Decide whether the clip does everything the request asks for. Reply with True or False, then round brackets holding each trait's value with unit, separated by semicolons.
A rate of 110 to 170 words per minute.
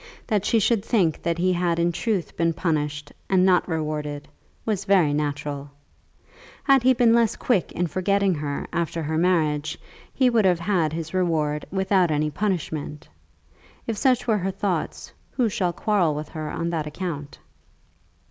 True (165 wpm)